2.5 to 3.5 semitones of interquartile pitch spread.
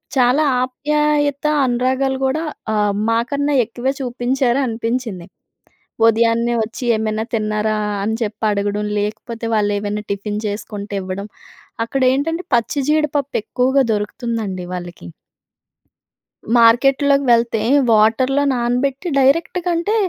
No: average, 4.3 semitones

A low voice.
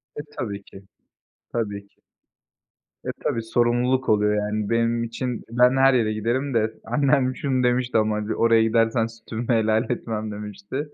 Yes: low, 115 Hz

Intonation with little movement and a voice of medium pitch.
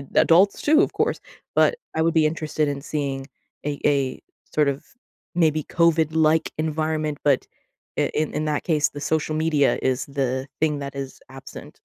Yes: narrow, 2.2 semitones; medium, 150 Hz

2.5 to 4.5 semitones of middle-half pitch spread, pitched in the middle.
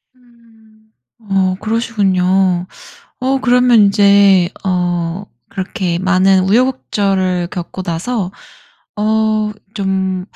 No: average, 2.9 semitones; high, 195 Hz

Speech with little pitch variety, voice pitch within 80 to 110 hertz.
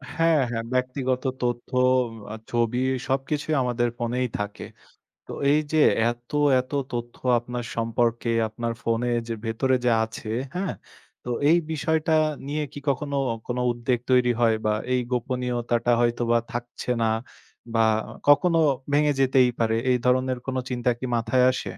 No: narrow, 1.9 semitones; low, 125 Hz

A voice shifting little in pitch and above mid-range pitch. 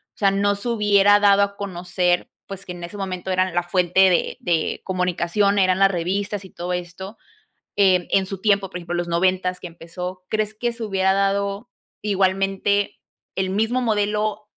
Yes: narrow, 2.0 semitones; high, 195 Hz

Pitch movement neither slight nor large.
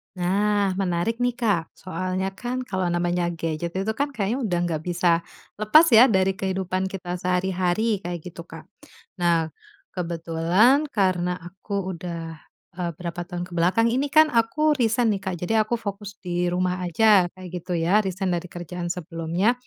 Yes: average, 3.4 semitones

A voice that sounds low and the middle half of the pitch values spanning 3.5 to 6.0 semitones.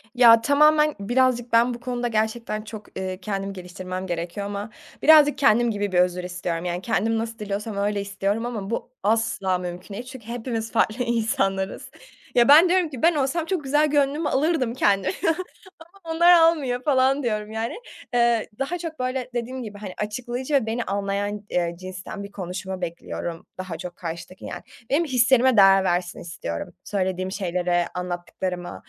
No: high, 220 Hz; average, 5.2 semitones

